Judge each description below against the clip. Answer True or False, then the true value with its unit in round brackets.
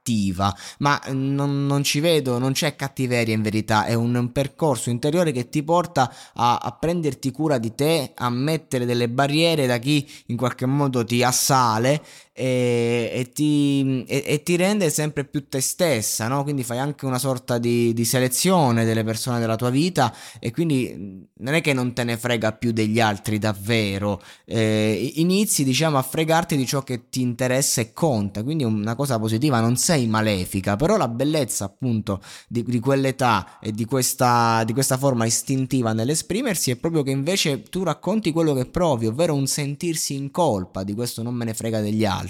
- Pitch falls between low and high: False (130 Hz)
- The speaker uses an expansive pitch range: False (4.0 semitones)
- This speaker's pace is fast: True (185 wpm)